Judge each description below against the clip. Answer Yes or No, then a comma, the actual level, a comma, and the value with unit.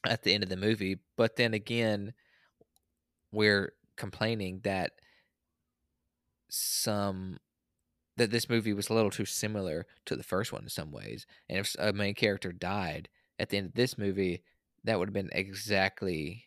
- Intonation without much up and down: No, average, 3.3 semitones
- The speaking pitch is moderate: No, low, 100 Hz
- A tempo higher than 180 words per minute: No, average, 165 wpm